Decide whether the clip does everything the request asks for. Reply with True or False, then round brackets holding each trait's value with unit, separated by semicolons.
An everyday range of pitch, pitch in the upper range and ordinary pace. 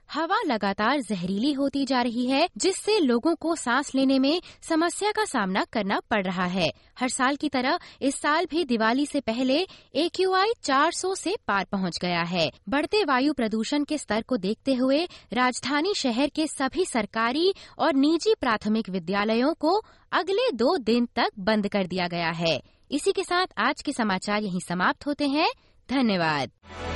False (7.2 semitones; 265 Hz; 170 wpm)